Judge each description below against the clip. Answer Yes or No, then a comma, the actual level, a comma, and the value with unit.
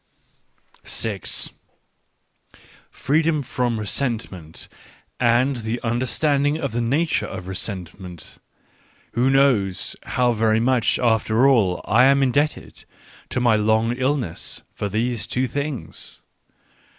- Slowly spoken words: Yes, slow, 115 wpm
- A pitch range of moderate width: Yes, average, 4.0 semitones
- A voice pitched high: No, low, 120 Hz